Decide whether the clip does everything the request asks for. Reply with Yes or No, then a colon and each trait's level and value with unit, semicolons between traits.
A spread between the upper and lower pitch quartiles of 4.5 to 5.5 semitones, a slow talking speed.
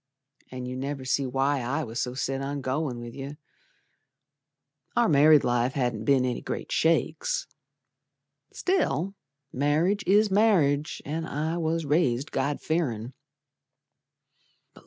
No: average, 4.0 semitones; slow, 125 wpm